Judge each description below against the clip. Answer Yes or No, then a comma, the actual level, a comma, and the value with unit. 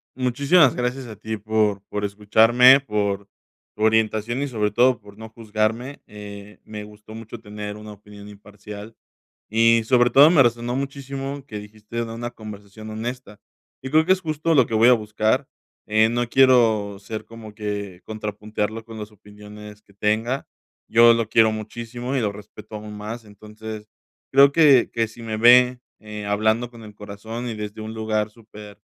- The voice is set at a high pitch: No, low, 110 Hz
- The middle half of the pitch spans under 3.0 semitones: Yes, narrow, 2.4 semitones